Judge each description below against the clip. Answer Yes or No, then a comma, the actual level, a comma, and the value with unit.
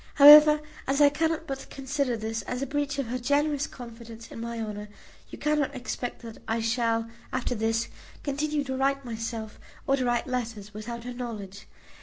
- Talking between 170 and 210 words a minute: Yes, average, 180 wpm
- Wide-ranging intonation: No, average, 3.7 semitones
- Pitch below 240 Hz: No, high, 245 Hz